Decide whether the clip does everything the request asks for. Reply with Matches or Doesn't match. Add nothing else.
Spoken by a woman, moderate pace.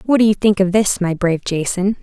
Doesn't match